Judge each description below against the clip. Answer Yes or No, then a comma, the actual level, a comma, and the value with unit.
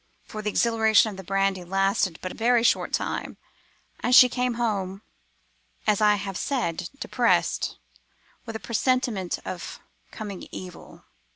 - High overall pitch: Yes, high, 210 Hz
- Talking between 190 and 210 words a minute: No, average, 145 wpm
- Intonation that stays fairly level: No, average, 3.3 semitones